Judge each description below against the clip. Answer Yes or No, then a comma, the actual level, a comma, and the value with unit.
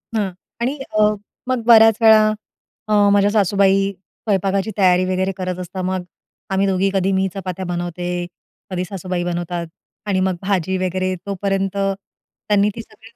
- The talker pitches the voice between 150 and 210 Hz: Yes, high, 190 Hz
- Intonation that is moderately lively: No, narrow, 1.6 semitones